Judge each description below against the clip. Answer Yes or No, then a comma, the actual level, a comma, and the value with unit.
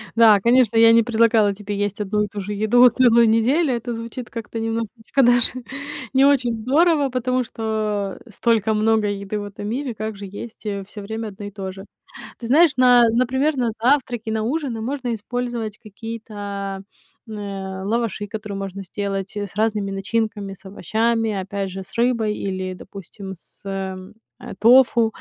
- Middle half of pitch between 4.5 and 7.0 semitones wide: No, average, 2.9 semitones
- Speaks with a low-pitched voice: No, high, 220 Hz